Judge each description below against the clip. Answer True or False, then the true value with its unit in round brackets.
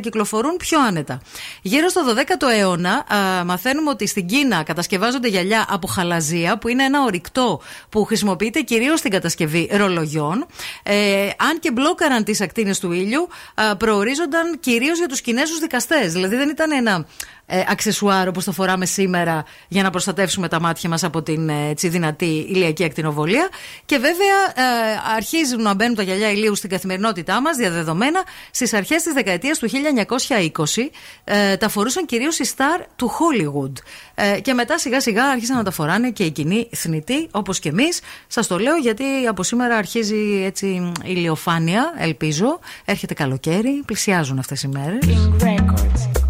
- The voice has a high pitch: True (210 Hz)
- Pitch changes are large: True (6.6 semitones)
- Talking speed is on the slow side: False (155 wpm)